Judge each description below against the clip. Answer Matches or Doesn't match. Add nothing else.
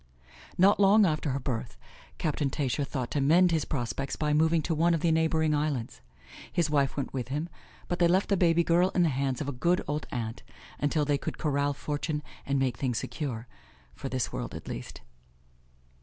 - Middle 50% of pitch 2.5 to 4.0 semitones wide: Matches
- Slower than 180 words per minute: Doesn't match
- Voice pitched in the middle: Matches